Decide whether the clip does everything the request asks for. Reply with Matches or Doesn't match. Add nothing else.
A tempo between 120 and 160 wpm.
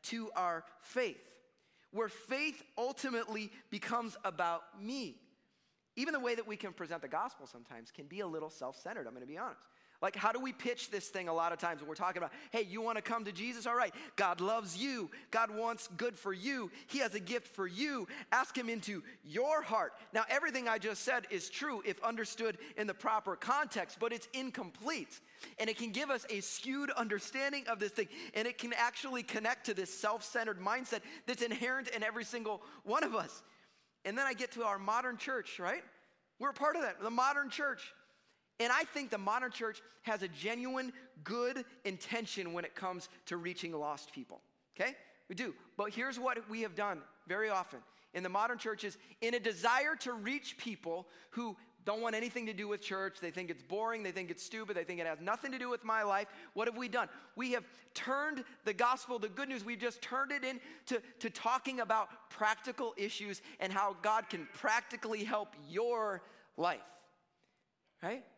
Doesn't match